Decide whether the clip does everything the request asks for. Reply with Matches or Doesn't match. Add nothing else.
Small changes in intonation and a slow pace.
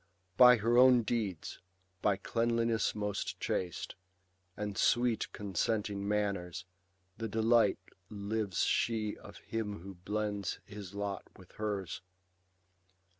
Matches